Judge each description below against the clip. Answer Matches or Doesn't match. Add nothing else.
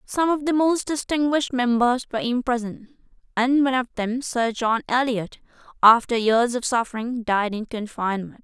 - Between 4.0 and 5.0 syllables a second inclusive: Doesn't match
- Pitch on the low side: Doesn't match